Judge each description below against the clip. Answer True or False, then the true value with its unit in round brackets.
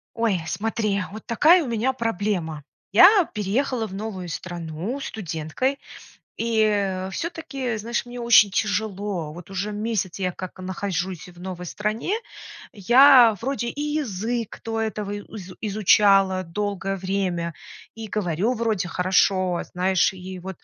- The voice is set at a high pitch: True (205 Hz)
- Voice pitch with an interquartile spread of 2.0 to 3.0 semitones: False (3.7 semitones)